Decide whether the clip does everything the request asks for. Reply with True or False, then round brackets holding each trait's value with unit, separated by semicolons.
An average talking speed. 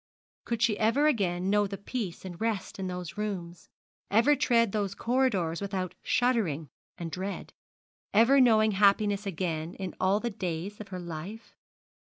True (150 wpm)